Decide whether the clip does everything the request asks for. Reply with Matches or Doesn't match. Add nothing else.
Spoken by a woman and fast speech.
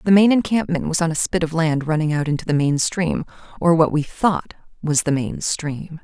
Matches